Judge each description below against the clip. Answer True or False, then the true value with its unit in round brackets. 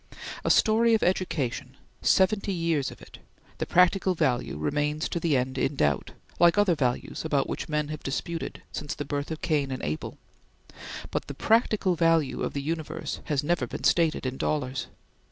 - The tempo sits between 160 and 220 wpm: True (175 wpm)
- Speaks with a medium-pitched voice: True (155 Hz)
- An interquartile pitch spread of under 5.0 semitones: True (4.1 semitones)